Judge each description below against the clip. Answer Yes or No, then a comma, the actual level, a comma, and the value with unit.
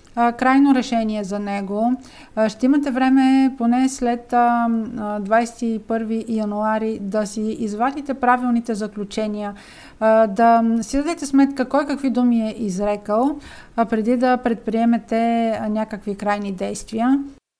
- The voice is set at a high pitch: Yes, high, 230 Hz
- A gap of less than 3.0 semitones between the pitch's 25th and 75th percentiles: Yes, narrow, 2.6 semitones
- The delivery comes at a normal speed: No, slow, 105 wpm